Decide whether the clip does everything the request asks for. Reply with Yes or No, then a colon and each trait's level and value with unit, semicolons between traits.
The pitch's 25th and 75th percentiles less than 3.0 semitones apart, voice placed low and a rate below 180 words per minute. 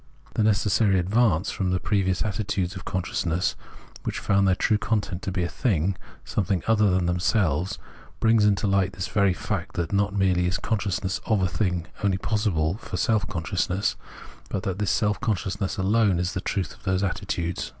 No: narrow, 2.4 semitones; very low, 95 Hz; average, 185 wpm